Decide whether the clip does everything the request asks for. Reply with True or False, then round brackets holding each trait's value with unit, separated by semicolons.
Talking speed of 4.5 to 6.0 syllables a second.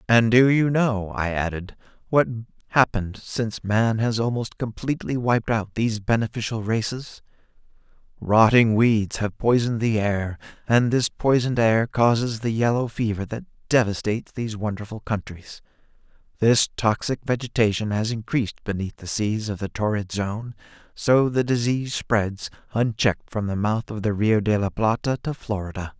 True (5.0 syllables/s)